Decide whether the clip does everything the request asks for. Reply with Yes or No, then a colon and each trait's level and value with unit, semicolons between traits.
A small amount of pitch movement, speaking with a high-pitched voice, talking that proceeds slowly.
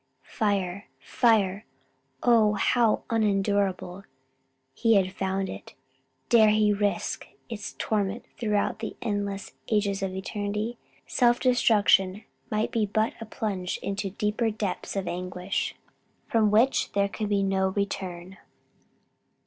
Yes: narrow, 2.0 semitones; high, 205 Hz; slow, 120 wpm